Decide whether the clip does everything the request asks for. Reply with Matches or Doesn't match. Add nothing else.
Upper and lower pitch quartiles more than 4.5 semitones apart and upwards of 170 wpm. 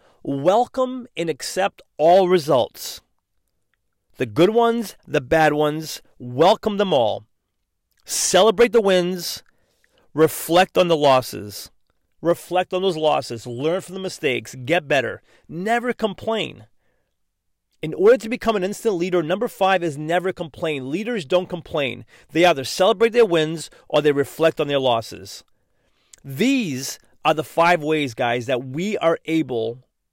Doesn't match